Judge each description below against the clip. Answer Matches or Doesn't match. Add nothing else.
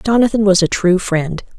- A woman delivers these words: Matches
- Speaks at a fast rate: Doesn't match